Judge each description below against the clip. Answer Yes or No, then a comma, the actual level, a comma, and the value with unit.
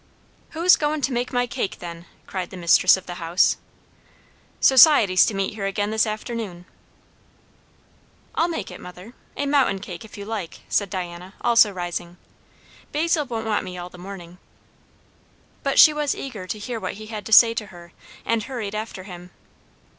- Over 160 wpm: Yes, average, 175 wpm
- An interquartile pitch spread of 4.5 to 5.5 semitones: Yes, average, 4.9 semitones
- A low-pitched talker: No, high, 210 Hz